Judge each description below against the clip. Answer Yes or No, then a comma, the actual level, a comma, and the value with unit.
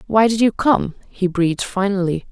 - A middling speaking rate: Yes, average, 180 wpm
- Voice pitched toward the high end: Yes, high, 195 Hz